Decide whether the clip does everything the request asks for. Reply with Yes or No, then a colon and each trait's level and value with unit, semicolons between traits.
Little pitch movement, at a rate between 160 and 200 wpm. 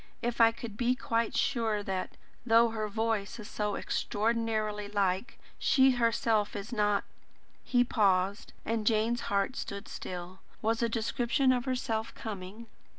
No: narrow, 2.3 semitones; average, 150 wpm